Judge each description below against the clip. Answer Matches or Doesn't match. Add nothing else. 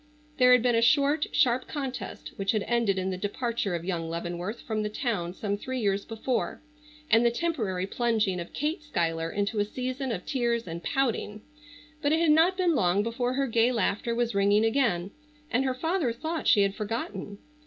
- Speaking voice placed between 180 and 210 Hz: Doesn't match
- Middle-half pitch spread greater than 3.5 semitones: Matches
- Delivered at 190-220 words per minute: Matches